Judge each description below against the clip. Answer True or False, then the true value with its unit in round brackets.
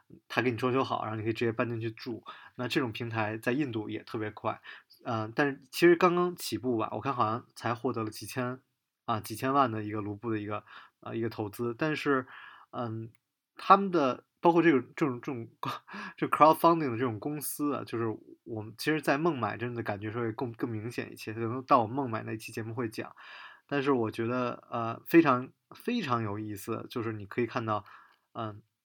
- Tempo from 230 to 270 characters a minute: False (325 characters per minute)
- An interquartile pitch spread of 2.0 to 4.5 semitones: True (3.5 semitones)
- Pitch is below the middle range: True (120 Hz)